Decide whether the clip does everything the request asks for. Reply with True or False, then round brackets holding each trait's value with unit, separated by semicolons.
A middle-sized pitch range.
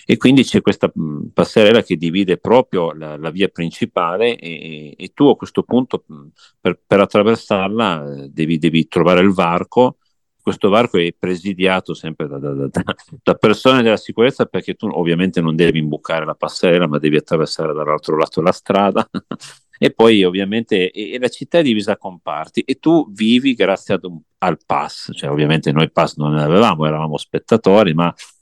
True (4.3 semitones)